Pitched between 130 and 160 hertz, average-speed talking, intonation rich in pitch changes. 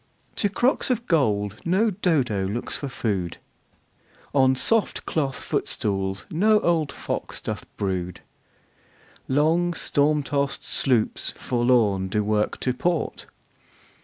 No: low, 135 Hz; slow, 115 wpm; wide, 8.2 semitones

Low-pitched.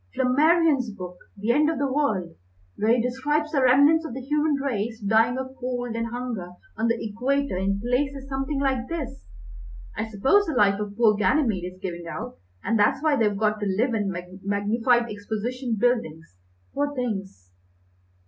No: high, 240 Hz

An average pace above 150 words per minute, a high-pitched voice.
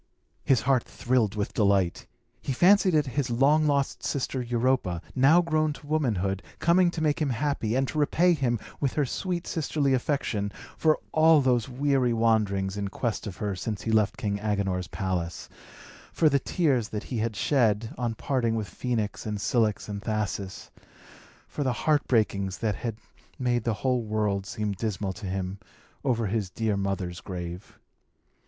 No: average, 170 wpm; low, 115 Hz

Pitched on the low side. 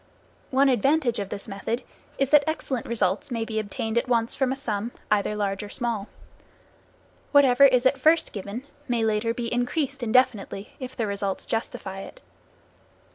No: high, 235 Hz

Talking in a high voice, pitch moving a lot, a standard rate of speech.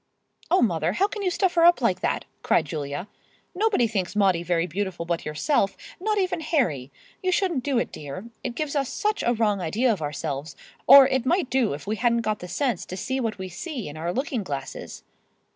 No: high, 225 Hz; wide, 8.8 semitones; fast, 210 wpm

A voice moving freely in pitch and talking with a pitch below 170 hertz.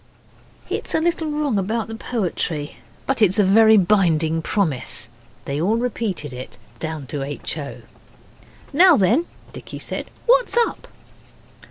No: wide, 7.8 semitones; high, 205 Hz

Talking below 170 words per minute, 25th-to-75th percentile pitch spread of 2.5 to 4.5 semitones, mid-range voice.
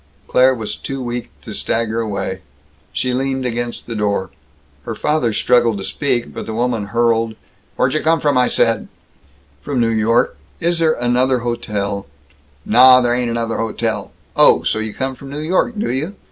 No: average, 160 wpm; average, 3.0 semitones; low, 120 Hz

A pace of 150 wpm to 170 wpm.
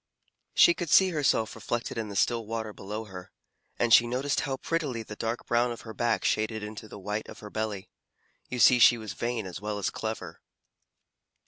No: average, 200 wpm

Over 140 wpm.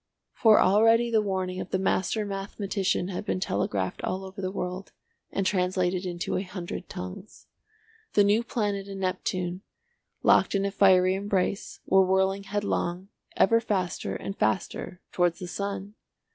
Yes: average, 150 wpm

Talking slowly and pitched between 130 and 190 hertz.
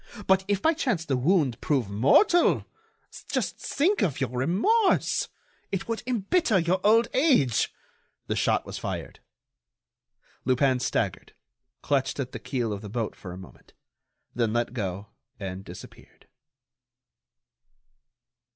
Yes: slow, 130 wpm; medium, 140 Hz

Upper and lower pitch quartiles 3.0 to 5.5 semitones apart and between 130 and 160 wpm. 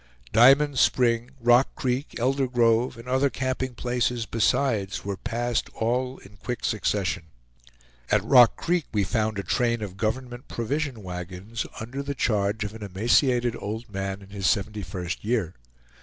Yes: average, 3.6 semitones; average, 155 wpm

